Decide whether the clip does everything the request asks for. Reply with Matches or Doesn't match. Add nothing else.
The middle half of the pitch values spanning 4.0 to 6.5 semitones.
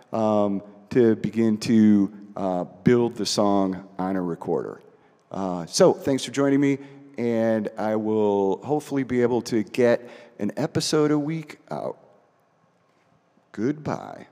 Matches